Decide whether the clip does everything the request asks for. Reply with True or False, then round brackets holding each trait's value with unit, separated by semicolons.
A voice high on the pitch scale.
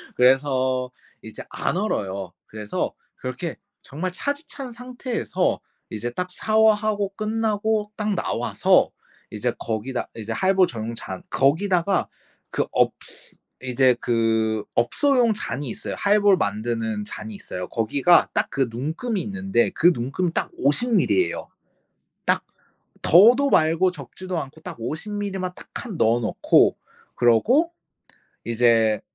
False (160 Hz)